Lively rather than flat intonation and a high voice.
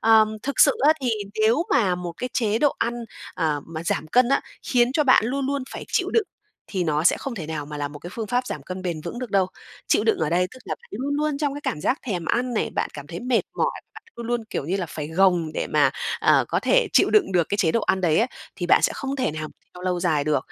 Yes: wide, 7.2 semitones; high, 200 Hz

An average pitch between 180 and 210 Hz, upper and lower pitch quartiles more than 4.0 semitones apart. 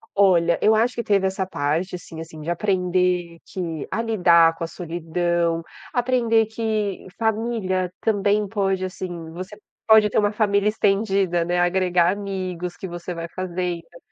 No: medium, 185 Hz; average, 3.2 semitones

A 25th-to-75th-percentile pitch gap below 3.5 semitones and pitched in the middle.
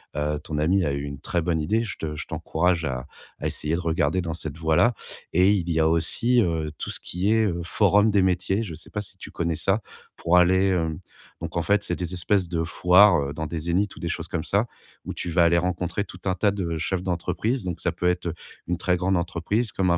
No: average, 2.9 semitones; very low, 90 Hz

